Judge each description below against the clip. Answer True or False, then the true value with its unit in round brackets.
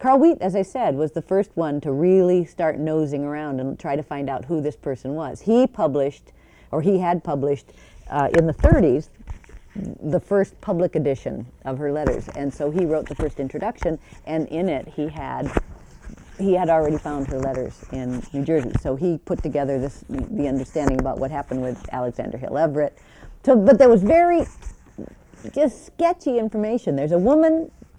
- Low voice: False (155 Hz)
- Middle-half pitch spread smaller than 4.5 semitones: False (5.2 semitones)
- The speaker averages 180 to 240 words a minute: True (185 wpm)